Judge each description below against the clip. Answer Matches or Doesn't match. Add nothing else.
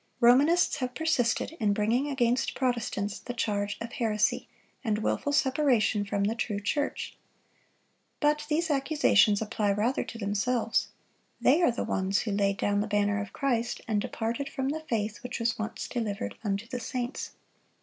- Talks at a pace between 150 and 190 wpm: Matches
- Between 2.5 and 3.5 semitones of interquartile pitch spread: Doesn't match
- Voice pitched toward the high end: Matches